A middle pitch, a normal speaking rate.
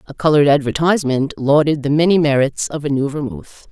Yes: medium, 145 Hz; average, 180 wpm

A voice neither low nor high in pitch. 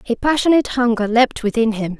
No: high, 235 Hz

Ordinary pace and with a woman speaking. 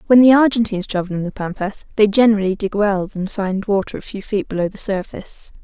No: fast, 215 wpm; female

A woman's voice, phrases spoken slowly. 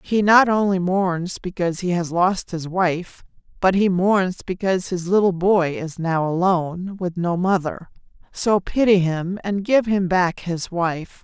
No: female; average, 170 wpm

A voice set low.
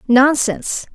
No: very high, 265 Hz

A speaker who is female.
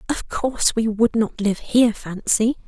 Yes: female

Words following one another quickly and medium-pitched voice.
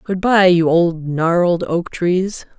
No: average, 140 wpm; medium, 175 Hz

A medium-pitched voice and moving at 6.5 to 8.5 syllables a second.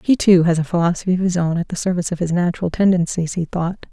Yes: medium, 175 Hz; 6.8 syllables/s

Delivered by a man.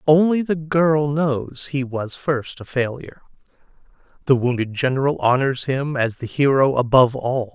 Yes: male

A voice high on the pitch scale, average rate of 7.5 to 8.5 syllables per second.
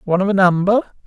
Yes: high, 195 Hz; 8.3 syllables/s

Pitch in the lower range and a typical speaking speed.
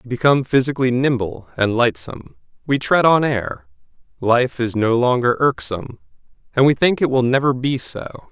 Yes: low, 125 Hz; average, 165 wpm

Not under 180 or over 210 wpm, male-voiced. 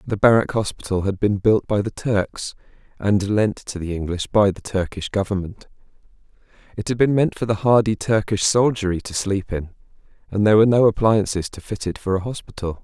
Yes: average, 190 wpm; male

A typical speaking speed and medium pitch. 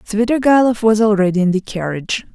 No: average, 155 wpm; high, 210 Hz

